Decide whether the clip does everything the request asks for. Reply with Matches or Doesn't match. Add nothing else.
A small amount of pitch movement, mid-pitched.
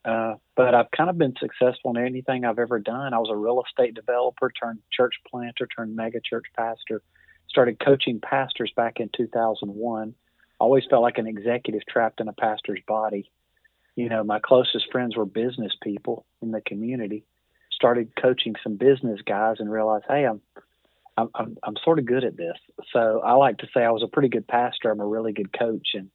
Doesn't match